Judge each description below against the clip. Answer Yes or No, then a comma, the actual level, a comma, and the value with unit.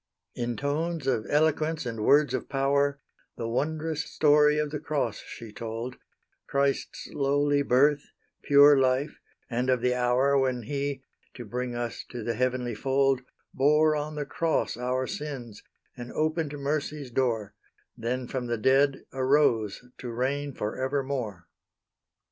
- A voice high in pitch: No, low, 135 Hz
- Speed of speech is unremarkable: Yes, average, 145 wpm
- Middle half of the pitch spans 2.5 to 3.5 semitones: Yes, average, 3.0 semitones